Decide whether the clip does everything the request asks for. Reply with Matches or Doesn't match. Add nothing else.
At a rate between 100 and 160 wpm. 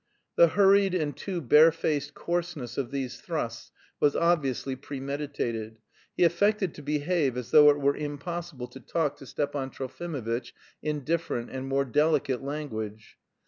Matches